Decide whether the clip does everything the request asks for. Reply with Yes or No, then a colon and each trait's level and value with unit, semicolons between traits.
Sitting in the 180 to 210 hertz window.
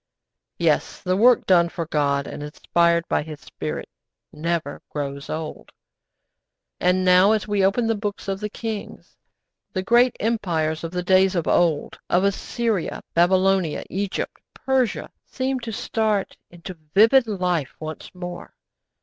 Yes: medium, 185 Hz